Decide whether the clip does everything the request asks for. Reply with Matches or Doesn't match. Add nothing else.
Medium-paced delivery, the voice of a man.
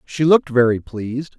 Matches